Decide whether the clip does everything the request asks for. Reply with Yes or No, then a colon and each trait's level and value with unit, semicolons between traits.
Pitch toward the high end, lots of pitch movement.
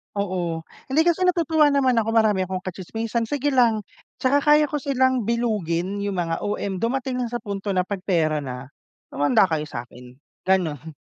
Yes: high, 205 Hz; wide, 7.0 semitones